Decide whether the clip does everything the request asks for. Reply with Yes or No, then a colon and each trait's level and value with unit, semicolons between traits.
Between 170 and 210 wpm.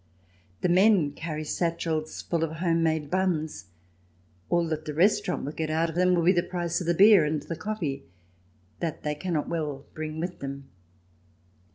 Yes: average, 180 wpm